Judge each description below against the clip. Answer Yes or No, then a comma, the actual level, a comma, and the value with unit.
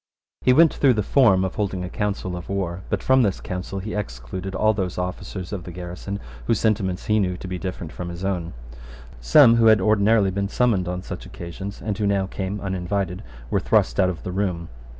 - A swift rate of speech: Yes, fast, 210 wpm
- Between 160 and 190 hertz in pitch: No, very low, 95 Hz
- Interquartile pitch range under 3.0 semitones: Yes, narrow, 2.4 semitones